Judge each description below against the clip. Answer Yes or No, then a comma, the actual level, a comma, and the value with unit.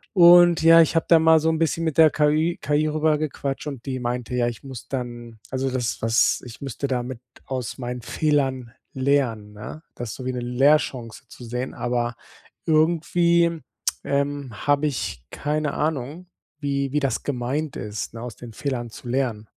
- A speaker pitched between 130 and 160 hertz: Yes, low, 135 Hz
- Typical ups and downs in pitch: Yes, average, 4.1 semitones